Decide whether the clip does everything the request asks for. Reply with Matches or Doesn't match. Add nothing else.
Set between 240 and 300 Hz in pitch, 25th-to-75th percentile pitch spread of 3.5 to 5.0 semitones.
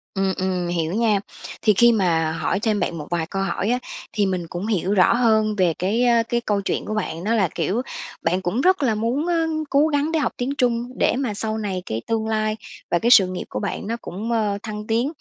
Doesn't match